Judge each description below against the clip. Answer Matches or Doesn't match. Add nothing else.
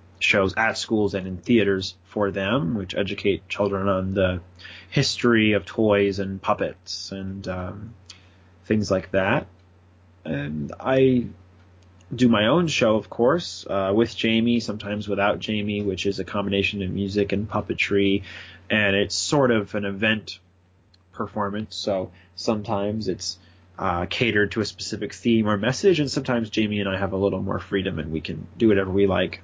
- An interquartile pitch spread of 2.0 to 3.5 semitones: Matches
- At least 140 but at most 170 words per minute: Matches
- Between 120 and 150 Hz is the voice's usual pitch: Doesn't match